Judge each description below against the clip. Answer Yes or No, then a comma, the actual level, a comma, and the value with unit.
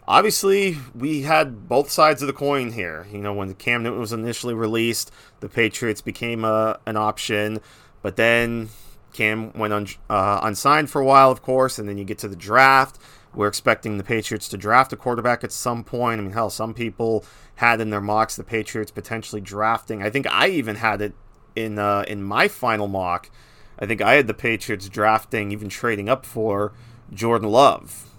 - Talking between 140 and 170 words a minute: No, average, 195 wpm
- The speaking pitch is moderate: No, low, 115 Hz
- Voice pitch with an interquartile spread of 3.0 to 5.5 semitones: No, narrow, 2.6 semitones